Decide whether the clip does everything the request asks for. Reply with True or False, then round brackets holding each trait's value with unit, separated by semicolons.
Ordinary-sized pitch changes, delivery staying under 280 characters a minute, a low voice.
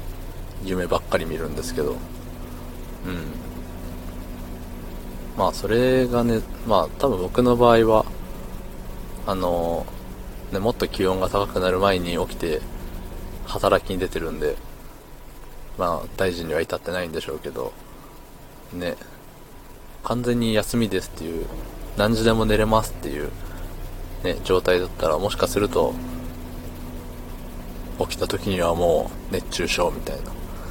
True (3.2 semitones; 250 characters per minute; 90 Hz)